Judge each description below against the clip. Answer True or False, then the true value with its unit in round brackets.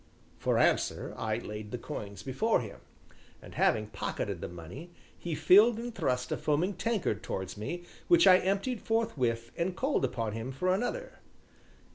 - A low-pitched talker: False (155 Hz)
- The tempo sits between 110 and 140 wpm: False (160 wpm)